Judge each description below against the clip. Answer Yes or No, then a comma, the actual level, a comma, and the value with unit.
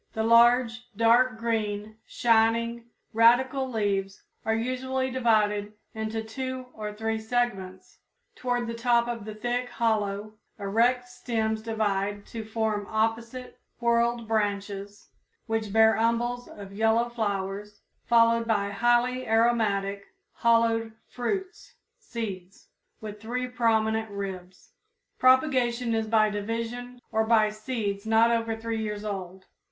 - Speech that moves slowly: Yes, slow, 115 wpm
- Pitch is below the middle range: No, high, 225 Hz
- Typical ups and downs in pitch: No, narrow, 2.2 semitones